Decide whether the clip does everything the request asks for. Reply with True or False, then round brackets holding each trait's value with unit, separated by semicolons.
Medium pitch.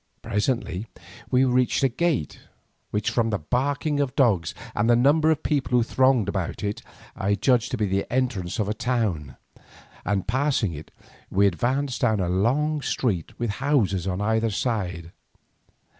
False (115 Hz)